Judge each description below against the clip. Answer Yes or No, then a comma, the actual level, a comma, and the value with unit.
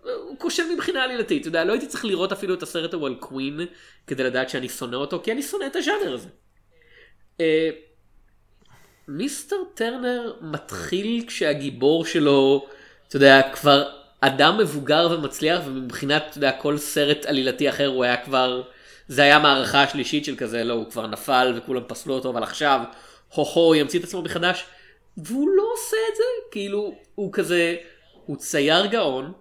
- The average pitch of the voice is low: No, medium, 150 Hz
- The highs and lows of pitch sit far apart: Yes, wide, 6.7 semitones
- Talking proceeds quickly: Yes, fast, 165 wpm